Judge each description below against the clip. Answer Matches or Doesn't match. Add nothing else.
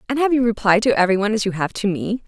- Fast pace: Matches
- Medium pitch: Doesn't match